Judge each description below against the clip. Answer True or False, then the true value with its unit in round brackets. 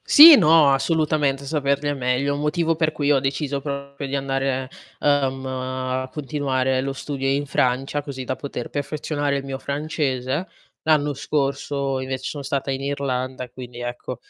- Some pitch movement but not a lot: False (1.7 semitones)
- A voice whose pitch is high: False (140 Hz)